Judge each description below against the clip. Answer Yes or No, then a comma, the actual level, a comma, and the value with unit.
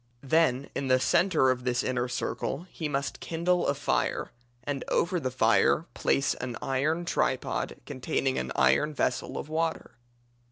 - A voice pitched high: No, low, 135 Hz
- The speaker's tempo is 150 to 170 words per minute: Yes, average, 155 wpm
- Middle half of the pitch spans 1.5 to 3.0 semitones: No, average, 4.1 semitones